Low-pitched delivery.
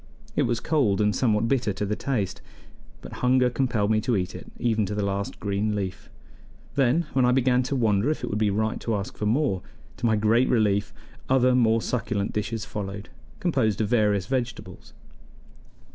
Yes: low, 110 Hz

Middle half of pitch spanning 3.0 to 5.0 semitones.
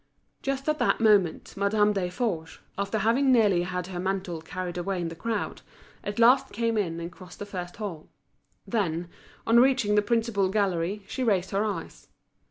Yes: average, 4.0 semitones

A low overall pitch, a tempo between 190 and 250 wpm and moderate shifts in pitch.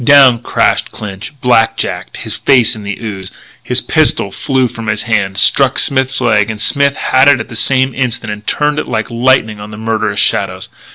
Yes: low, 115 Hz; average, 195 wpm; average, 3.6 semitones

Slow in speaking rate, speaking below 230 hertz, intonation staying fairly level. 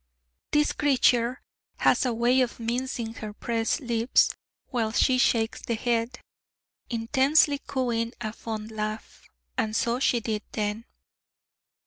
No: slow, 125 wpm; high, 235 Hz; narrow, 2.2 semitones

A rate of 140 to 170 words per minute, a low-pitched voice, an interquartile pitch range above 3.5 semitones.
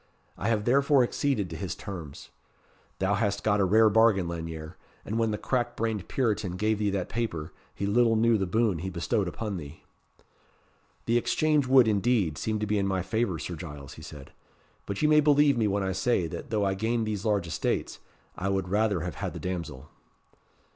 No: average, 200 wpm; low, 105 Hz; average, 4.1 semitones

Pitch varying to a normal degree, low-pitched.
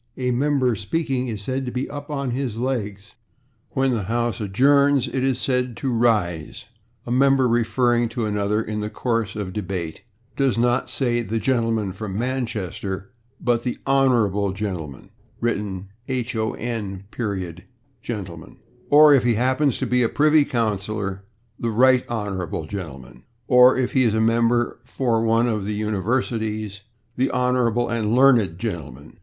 Yes: average, 3.7 semitones; low, 115 Hz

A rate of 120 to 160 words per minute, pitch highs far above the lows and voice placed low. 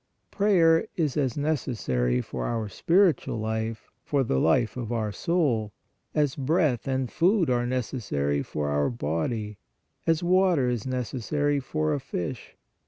Yes: average, 145 wpm; wide, 6.0 semitones; low, 125 Hz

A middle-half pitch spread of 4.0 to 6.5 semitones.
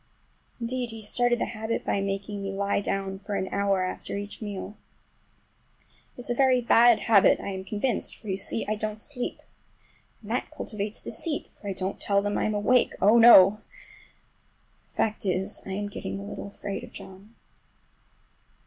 No: average, 2.7 semitones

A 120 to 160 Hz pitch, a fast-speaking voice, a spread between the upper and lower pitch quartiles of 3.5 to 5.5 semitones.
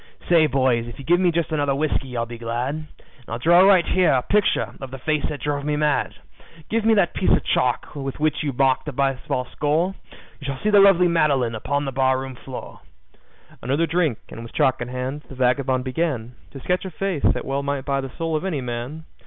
Yes: medium, 140 Hz; fast, 225 wpm; average, 4.0 semitones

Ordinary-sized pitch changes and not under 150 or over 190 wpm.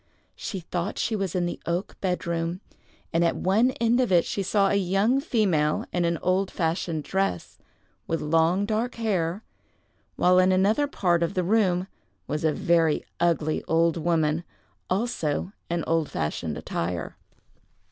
Yes: average, 3.2 semitones; average, 155 wpm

